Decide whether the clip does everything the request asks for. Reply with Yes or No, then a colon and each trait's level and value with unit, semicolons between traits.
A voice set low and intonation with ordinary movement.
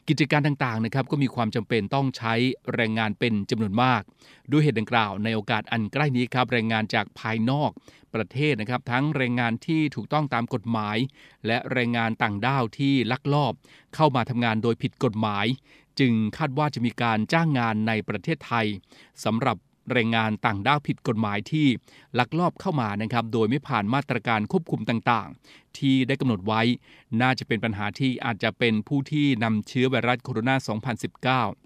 Yes: low, 120 Hz; average, 3.5 semitones